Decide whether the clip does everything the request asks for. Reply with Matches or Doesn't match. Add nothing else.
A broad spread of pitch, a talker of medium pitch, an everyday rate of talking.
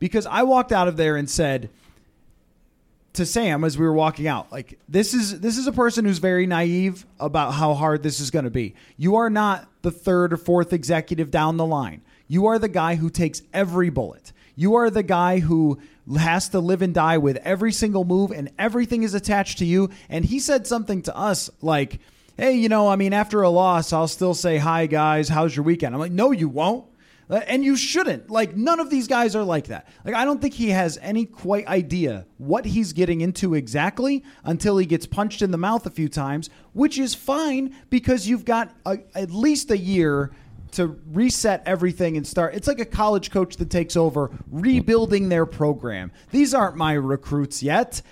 Doesn't match